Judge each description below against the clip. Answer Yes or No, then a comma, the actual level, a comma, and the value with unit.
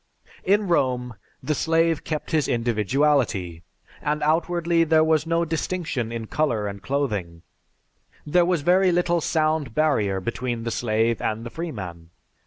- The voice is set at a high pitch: No, medium, 145 Hz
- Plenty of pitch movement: Yes, wide, 6.4 semitones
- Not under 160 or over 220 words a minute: No, average, 145 wpm